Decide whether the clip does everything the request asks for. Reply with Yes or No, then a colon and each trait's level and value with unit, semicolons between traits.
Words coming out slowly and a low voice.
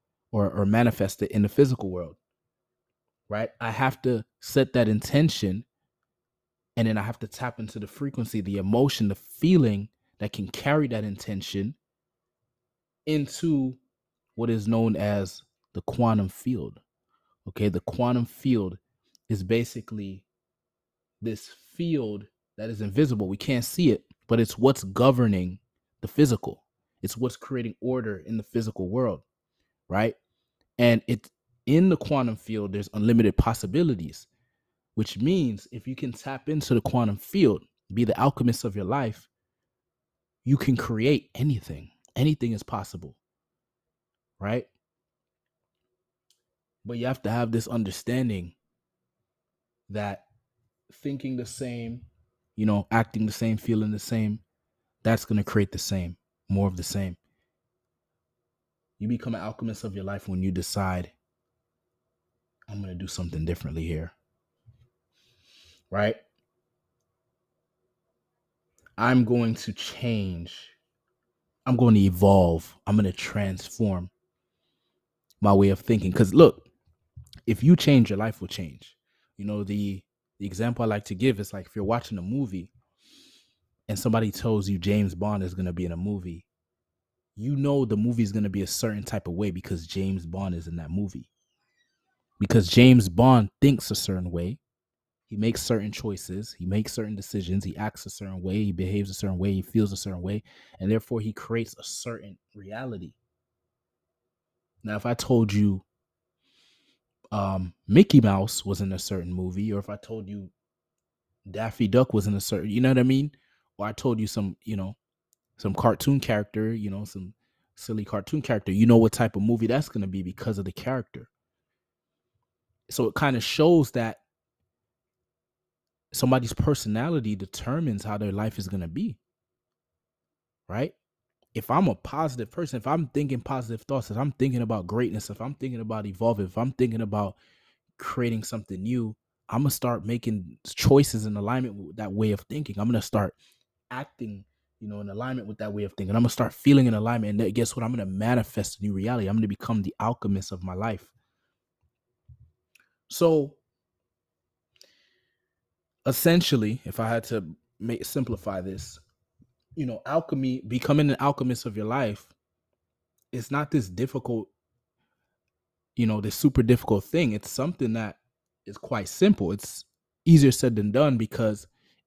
No: average, 160 wpm; low, 110 Hz